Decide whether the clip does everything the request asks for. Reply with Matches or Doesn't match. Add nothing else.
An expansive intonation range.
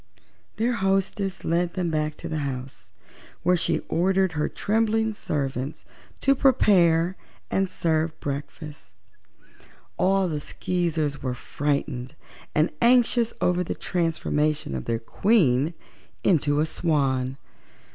Doesn't match